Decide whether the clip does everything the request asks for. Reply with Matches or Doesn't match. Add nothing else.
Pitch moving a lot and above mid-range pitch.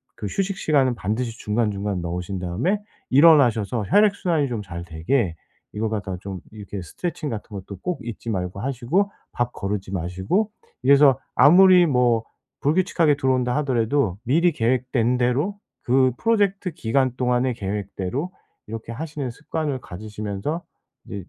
Doesn't match